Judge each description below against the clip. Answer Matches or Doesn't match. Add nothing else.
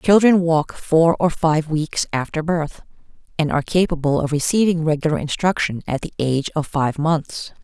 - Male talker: Doesn't match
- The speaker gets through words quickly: Doesn't match